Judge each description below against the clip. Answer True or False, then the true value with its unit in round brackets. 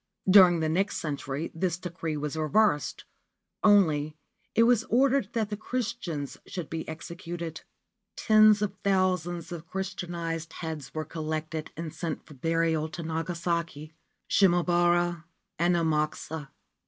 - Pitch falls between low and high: True (170 Hz)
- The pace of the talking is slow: True (125 wpm)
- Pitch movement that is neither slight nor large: True (3.0 semitones)